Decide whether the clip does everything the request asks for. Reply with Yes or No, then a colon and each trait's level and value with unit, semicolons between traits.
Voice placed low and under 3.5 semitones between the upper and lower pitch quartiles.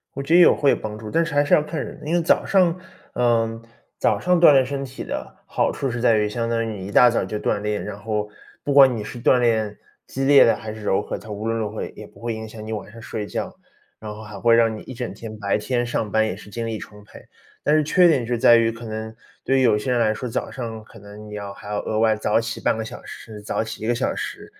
Yes: low, 115 Hz; average, 2.8 semitones